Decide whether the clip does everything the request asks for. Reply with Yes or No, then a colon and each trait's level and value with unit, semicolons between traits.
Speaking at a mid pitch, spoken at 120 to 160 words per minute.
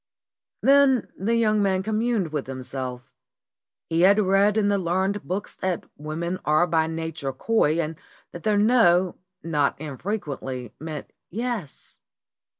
Yes: medium, 175 Hz; average, 140 wpm